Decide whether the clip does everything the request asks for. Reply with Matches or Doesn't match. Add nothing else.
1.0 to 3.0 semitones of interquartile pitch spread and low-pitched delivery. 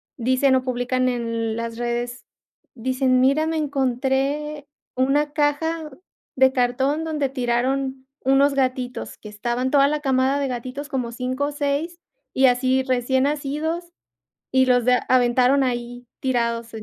Doesn't match